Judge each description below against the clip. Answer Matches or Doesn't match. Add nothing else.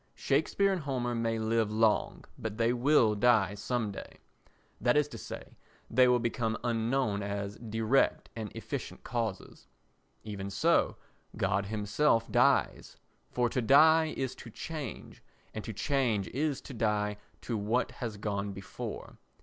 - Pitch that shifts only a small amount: Doesn't match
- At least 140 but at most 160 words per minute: Matches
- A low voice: Matches